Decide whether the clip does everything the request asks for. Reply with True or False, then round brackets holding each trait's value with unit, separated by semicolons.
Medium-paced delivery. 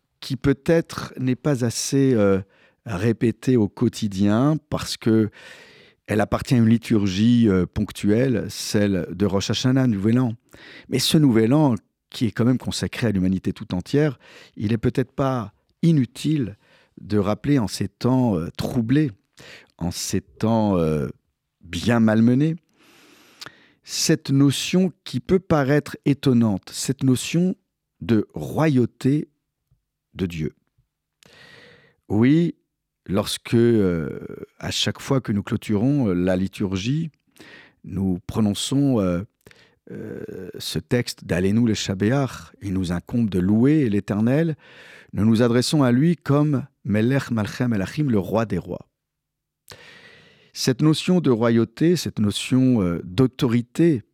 False (125 wpm)